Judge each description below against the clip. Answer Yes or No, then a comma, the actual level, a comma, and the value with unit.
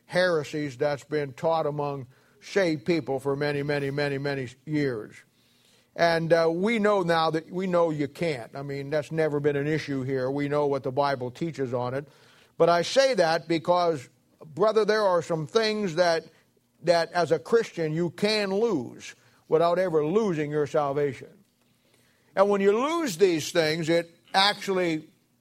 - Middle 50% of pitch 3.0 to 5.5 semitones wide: Yes, average, 3.6 semitones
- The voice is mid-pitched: Yes, medium, 160 Hz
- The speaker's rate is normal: Yes, average, 165 wpm